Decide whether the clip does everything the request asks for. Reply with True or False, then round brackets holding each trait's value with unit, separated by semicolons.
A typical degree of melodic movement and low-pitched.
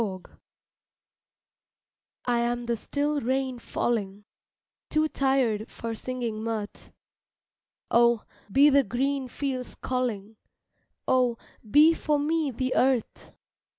False (3.2 semitones; 250 Hz)